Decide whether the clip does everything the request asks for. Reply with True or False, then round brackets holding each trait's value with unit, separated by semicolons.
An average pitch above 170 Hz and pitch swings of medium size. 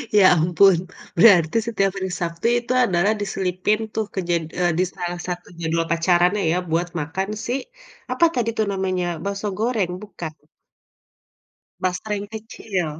True (185 Hz; 3.0 semitones)